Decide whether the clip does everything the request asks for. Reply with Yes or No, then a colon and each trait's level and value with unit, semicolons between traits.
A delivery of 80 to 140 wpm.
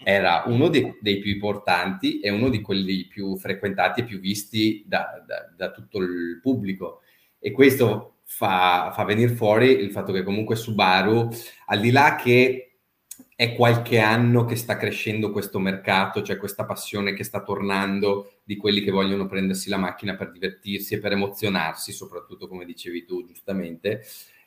No: average, 165 wpm